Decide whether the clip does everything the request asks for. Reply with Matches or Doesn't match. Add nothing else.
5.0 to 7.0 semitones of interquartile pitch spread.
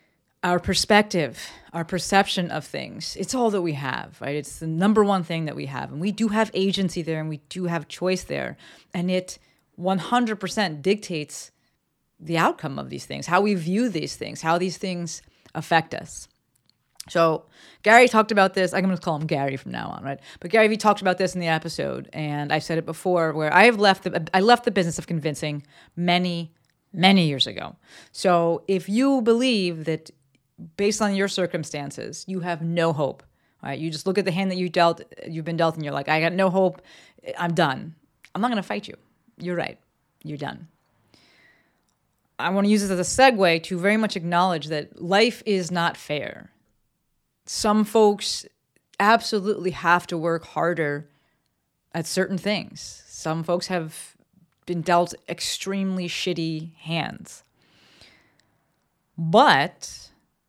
Doesn't match